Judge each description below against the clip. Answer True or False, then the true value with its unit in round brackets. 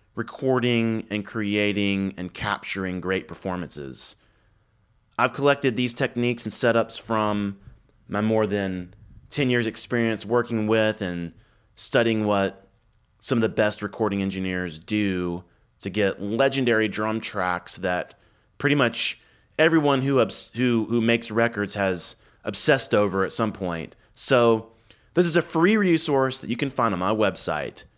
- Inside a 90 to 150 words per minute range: True (140 wpm)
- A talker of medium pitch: False (110 Hz)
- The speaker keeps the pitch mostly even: False (3.0 semitones)